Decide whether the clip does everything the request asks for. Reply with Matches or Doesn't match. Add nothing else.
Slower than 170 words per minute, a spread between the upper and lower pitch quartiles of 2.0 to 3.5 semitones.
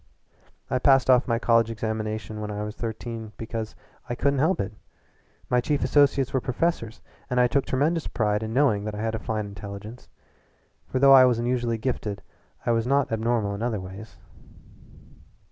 Doesn't match